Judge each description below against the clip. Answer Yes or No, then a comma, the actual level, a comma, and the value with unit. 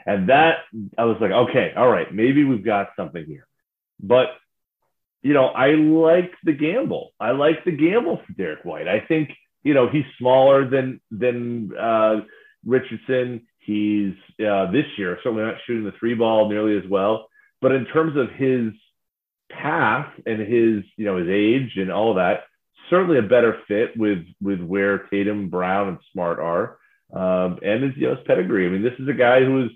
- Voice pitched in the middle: No, low, 115 Hz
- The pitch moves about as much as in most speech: Yes, average, 4.1 semitones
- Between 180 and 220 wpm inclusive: Yes, average, 190 wpm